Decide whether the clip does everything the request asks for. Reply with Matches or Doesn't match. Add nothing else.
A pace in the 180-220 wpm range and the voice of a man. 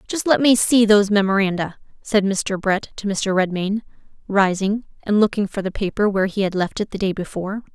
Doesn't match